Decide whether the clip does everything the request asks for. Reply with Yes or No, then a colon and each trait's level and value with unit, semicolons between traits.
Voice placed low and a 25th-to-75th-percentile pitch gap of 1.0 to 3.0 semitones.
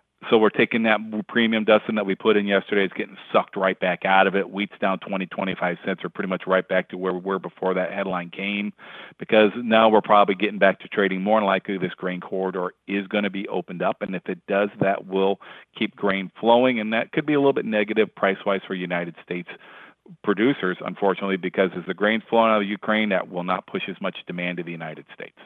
Yes: low, 100 Hz; narrow, 2.6 semitones